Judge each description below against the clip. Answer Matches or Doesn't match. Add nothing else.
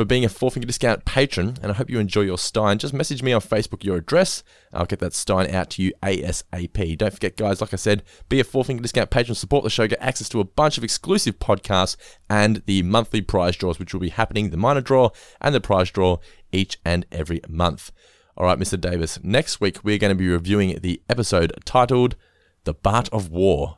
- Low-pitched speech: Matches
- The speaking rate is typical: Doesn't match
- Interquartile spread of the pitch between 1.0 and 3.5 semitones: Doesn't match